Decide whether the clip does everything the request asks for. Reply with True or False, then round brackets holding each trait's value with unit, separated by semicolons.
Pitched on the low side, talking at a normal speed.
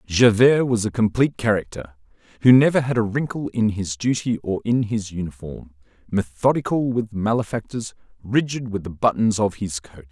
True (110 Hz; 160 wpm)